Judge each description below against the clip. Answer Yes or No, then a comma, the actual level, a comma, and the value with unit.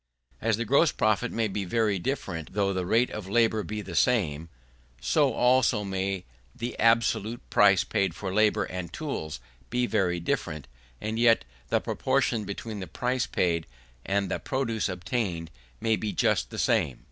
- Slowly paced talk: No, average, 165 wpm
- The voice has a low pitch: Yes, low, 105 Hz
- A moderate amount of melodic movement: Yes, average, 4.0 semitones